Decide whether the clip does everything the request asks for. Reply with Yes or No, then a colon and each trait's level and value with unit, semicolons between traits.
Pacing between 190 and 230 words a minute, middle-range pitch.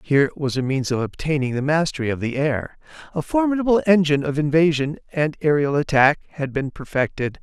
No: average, 180 wpm; medium, 150 Hz